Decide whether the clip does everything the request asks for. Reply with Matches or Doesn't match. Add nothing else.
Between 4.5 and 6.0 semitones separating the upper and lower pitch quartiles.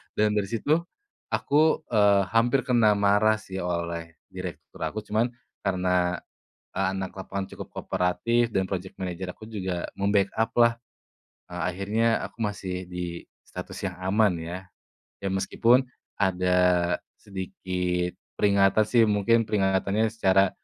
Doesn't match